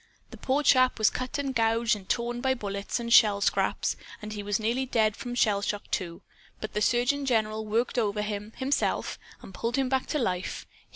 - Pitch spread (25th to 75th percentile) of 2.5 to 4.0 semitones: Yes, average, 3.3 semitones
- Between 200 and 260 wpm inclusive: Yes, fast, 205 wpm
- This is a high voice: Yes, high, 225 Hz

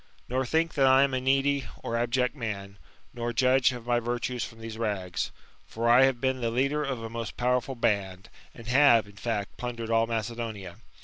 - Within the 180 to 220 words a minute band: Yes, average, 195 wpm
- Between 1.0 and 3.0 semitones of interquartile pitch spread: Yes, narrow, 2.5 semitones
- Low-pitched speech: Yes, low, 120 Hz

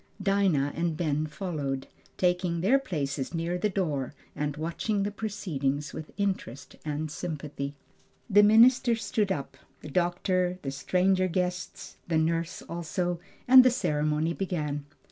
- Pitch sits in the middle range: Yes, medium, 170 Hz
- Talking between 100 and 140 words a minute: Yes, slow, 135 wpm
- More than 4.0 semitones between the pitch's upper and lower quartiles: Yes, average, 4.4 semitones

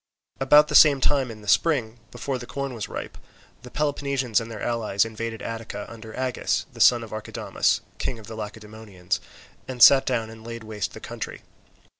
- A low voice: Yes, low, 115 Hz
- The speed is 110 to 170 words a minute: No, average, 185 wpm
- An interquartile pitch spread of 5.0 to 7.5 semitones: No, average, 3.1 semitones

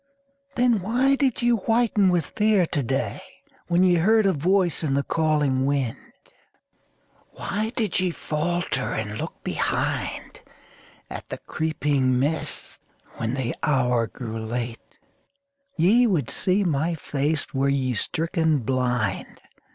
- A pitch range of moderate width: No, wide, 6.4 semitones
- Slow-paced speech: Yes, slow, 130 wpm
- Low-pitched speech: No, medium, 155 Hz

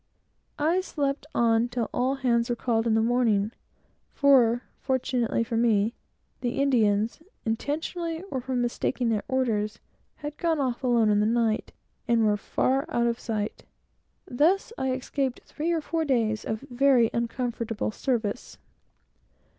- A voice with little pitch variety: No, average, 3.3 semitones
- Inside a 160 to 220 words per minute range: No, average, 145 wpm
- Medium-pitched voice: No, high, 240 Hz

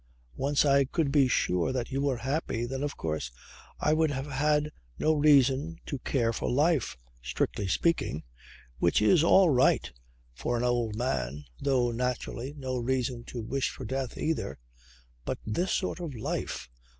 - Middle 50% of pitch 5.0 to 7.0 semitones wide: No, average, 3.6 semitones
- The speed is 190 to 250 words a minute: No, average, 160 wpm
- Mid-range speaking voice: No, low, 130 Hz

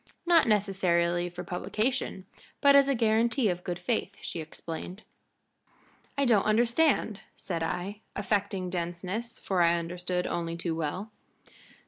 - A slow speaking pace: Yes, slow, 130 wpm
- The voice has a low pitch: No, high, 190 Hz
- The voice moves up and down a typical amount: Yes, average, 4.2 semitones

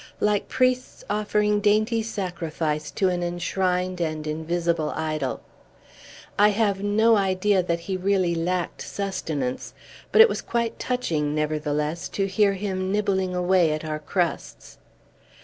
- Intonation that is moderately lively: Yes, average, 4.2 semitones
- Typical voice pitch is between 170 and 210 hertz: Yes, medium, 185 Hz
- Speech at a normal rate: No, slow, 130 wpm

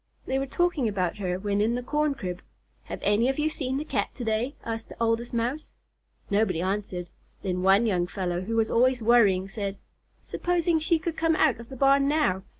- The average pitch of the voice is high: Yes, high, 230 Hz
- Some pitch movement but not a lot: No, wide, 5.9 semitones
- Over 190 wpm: Yes, fast, 205 wpm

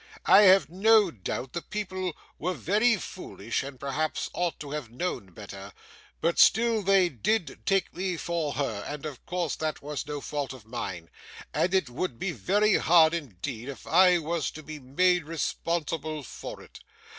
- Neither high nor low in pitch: Yes, medium, 160 Hz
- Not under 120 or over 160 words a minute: No, average, 170 wpm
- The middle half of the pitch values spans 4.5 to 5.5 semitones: Yes, average, 5.0 semitones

